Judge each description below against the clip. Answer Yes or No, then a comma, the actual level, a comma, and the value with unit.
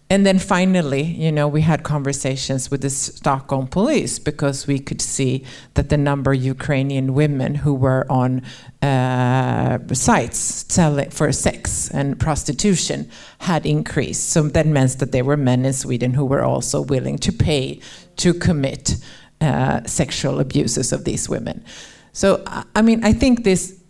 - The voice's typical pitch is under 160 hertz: Yes, medium, 140 Hz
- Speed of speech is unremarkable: Yes, average, 160 wpm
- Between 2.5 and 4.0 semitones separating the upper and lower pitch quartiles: Yes, average, 3.0 semitones